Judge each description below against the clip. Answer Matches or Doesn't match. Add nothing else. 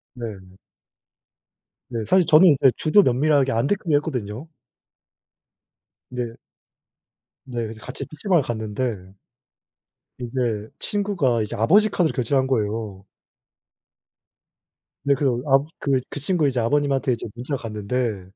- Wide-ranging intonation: Doesn't match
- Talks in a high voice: Doesn't match